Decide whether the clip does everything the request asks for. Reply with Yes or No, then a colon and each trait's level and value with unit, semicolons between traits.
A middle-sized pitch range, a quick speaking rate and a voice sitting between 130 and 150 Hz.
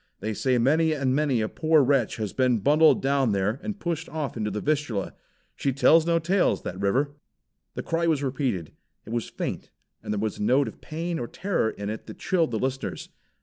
No: wide, 6.1 semitones; fast, 210 wpm; low, 135 Hz